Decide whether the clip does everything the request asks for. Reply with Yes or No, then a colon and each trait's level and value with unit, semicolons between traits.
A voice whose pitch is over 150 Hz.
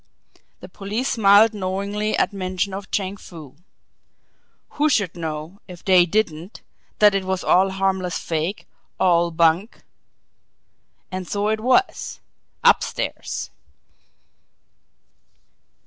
Yes: high, 190 Hz